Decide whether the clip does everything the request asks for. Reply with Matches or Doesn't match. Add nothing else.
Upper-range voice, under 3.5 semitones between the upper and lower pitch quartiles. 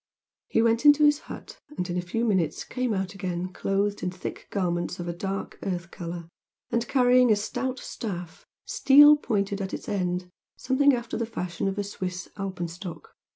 Doesn't match